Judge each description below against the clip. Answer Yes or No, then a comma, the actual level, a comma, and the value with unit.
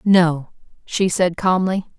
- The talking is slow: Yes, slow, 120 wpm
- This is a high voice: No, medium, 180 Hz